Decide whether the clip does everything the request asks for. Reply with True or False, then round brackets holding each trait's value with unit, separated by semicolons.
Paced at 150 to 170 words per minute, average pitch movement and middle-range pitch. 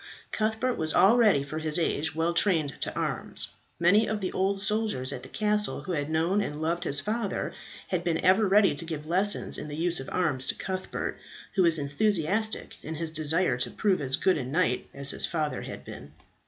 False (205 wpm; 4.8 semitones; 170 Hz)